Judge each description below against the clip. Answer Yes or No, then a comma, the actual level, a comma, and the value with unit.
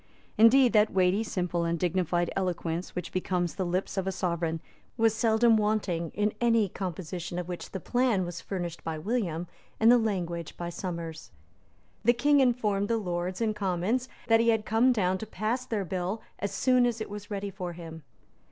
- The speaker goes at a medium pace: Yes, average, 185 wpm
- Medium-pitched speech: No, high, 195 Hz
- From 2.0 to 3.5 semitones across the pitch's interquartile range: No, average, 4.2 semitones